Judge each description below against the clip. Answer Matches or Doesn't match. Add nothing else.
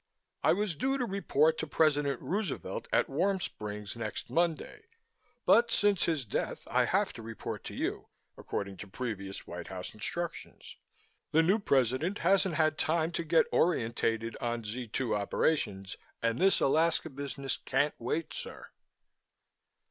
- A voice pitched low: Doesn't match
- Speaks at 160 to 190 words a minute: Doesn't match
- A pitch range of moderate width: Doesn't match